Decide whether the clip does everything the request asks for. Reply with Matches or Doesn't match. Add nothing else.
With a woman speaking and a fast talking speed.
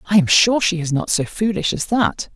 Matches